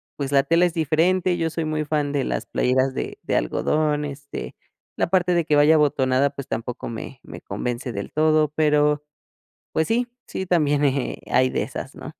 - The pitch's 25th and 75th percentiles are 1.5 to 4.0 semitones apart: Yes, average, 2.7 semitones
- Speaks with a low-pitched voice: No, medium, 150 Hz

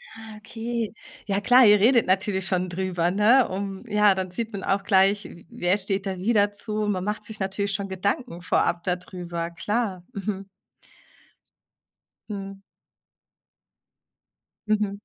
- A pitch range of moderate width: No, narrow, 2.0 semitones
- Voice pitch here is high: Yes, high, 200 Hz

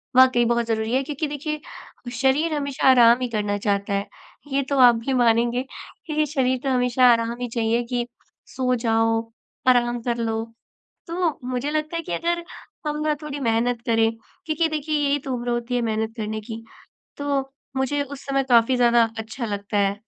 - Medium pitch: No, high, 245 Hz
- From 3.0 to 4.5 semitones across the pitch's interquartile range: Yes, average, 3.6 semitones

